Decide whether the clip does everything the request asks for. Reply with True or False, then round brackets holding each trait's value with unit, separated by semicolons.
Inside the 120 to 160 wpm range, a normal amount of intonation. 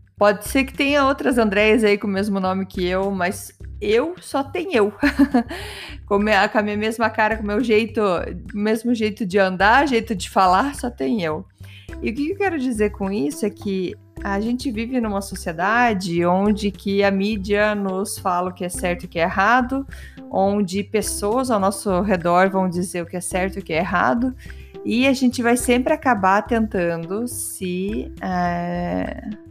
False (185 wpm; 4.1 semitones)